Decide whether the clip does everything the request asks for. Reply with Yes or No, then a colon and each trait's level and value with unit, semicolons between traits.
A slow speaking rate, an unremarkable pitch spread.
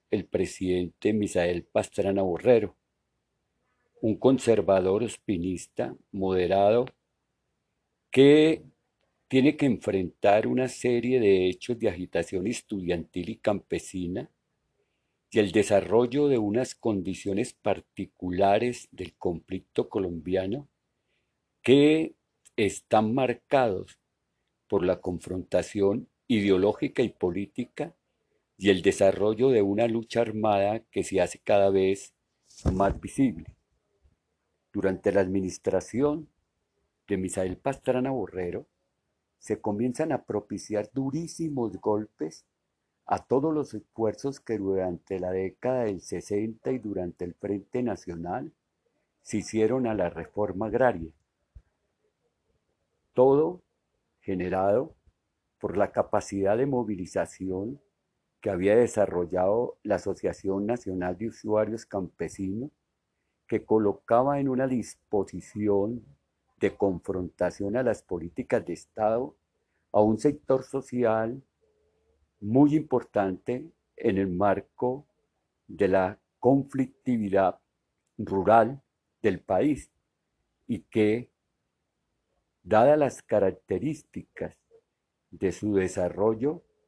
Yes: slow, 95 wpm; average, 4.9 semitones